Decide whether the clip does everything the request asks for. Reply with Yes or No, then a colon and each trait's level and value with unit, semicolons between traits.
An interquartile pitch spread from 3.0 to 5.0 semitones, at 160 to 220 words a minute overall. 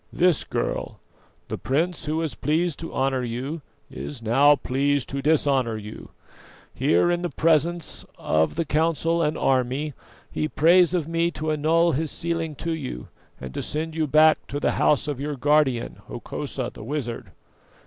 Yes: average, 3.5 semitones; average, 165 wpm